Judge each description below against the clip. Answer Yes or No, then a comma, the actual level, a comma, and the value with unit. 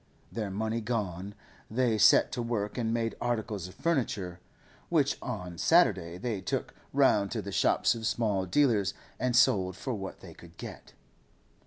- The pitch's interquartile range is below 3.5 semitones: No, average, 3.9 semitones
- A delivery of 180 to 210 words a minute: No, average, 160 wpm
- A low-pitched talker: Yes, low, 110 Hz